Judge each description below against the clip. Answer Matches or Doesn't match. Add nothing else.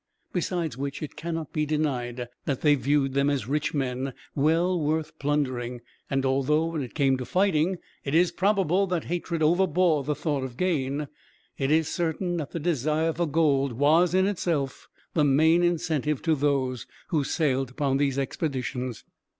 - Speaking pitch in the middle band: Matches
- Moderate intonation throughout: Matches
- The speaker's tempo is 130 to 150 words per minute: Doesn't match